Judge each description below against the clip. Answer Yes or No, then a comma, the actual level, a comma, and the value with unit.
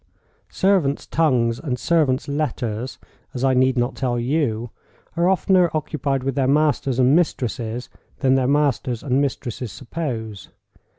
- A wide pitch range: No, average, 3.5 semitones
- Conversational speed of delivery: No, slow, 125 wpm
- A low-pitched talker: Yes, low, 130 Hz